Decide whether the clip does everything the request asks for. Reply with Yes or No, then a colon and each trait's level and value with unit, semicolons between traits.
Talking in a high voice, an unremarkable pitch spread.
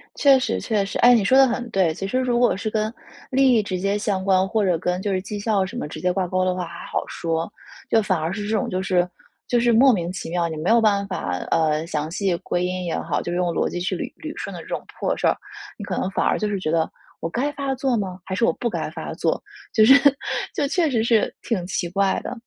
Yes: high, 195 Hz; average, 4.3 semitones